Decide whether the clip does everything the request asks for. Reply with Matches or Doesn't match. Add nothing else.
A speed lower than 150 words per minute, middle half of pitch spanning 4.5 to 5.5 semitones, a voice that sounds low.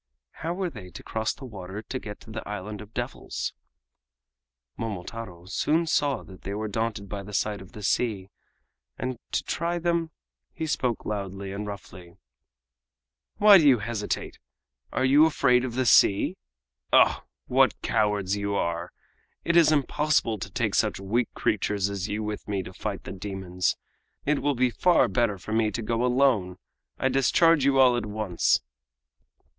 Doesn't match